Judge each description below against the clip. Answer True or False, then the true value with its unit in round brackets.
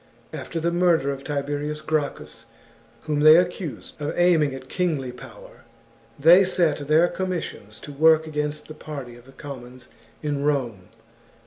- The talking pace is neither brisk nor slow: True (150 wpm)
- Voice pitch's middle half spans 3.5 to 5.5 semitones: False (3.0 semitones)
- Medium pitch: True (150 Hz)